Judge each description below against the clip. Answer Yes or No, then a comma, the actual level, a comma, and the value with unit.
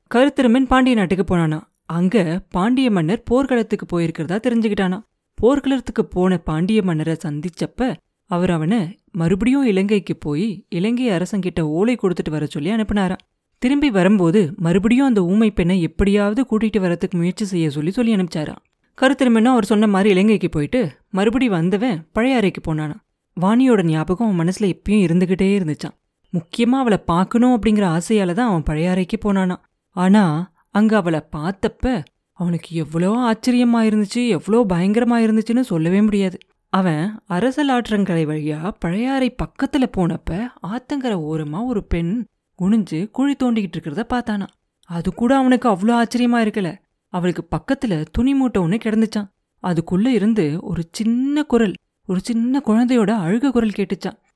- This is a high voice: Yes, high, 205 Hz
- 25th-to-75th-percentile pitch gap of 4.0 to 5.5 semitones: Yes, average, 5.0 semitones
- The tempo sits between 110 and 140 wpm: Yes, fast, 130 wpm